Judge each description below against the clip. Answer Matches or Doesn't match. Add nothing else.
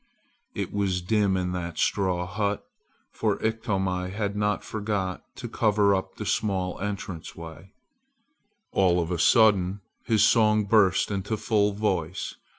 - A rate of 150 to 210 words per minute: Doesn't match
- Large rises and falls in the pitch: Doesn't match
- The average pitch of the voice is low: Matches